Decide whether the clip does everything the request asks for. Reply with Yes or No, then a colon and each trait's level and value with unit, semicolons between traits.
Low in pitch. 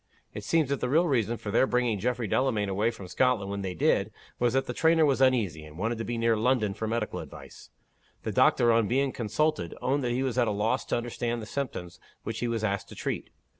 Yes: low, 115 Hz